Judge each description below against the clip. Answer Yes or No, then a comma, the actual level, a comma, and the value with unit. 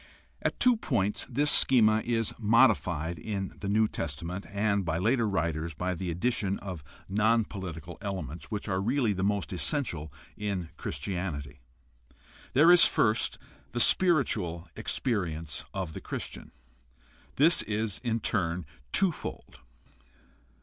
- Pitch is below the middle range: Yes, low, 100 Hz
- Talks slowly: Yes, slow, 130 wpm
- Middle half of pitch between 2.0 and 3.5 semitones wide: No, average, 5.0 semitones